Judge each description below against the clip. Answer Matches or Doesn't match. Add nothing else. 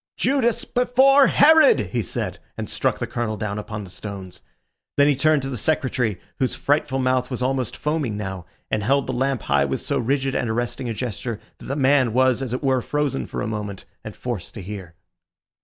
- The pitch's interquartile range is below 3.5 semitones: Doesn't match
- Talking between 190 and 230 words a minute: Matches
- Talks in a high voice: Doesn't match